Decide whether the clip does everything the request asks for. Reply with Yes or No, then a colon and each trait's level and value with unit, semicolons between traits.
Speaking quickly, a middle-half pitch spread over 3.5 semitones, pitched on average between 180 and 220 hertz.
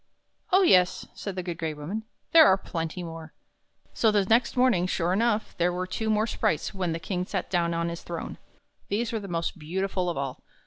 Yes: fast, 210 wpm; average, 4.0 semitones; medium, 185 Hz